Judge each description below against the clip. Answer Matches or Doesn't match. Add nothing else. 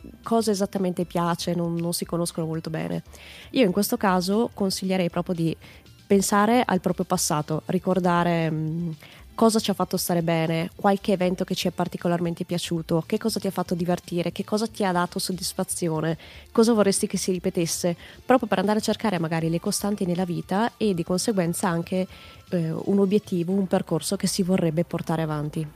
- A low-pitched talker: Doesn't match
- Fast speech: Matches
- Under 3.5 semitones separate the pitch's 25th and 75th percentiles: Matches